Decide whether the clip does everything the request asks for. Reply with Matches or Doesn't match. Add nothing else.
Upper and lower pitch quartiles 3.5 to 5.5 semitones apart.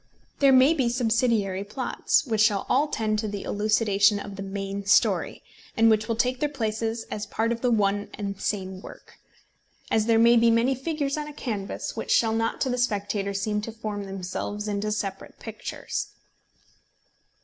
Doesn't match